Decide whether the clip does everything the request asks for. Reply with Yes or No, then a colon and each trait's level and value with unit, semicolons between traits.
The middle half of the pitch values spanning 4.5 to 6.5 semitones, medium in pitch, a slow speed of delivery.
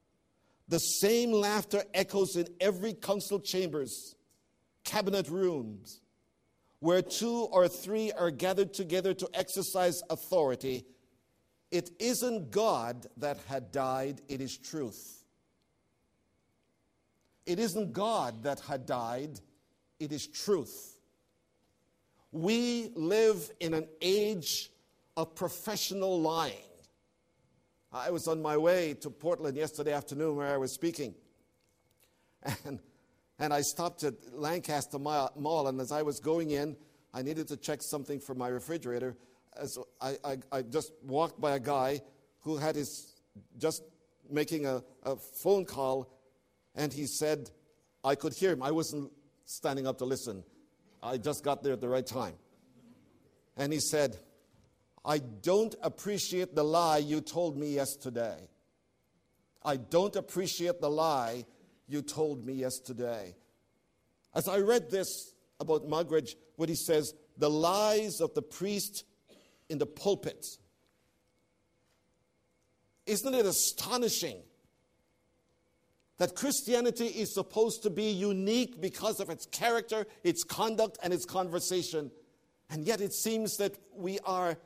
Yes: average, 5.2 semitones; medium, 160 Hz; slow, 130 wpm